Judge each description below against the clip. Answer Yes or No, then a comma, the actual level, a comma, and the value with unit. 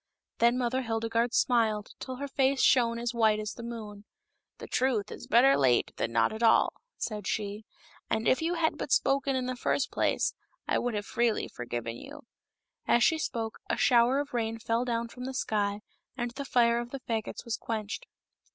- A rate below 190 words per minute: No, average, 200 wpm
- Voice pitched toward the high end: Yes, high, 235 Hz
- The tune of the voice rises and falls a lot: No, average, 2.8 semitones